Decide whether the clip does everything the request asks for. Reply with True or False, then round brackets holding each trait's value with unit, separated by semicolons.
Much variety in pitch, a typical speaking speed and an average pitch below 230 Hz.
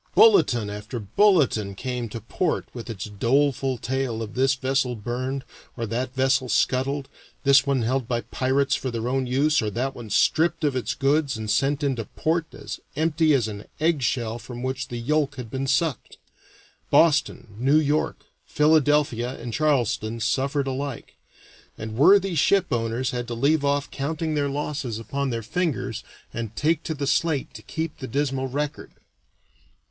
False (3.7 semitones; 165 wpm; 135 Hz)